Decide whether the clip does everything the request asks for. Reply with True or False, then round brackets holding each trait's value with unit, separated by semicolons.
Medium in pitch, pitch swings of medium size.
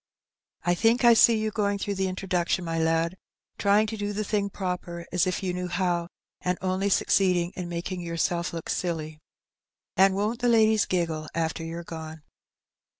True (180 Hz; 3.0 semitones)